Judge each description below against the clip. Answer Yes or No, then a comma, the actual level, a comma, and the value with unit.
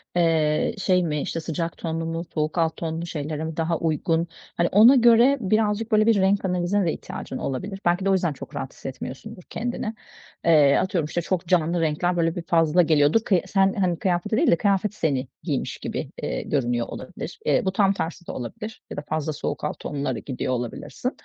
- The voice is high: No, medium, 170 Hz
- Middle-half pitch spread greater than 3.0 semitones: Yes, average, 4.0 semitones